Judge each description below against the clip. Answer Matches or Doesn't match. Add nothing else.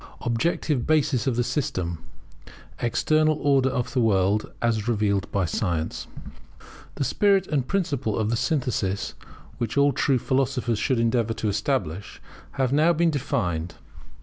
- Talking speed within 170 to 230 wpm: Doesn't match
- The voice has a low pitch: Matches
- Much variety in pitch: Doesn't match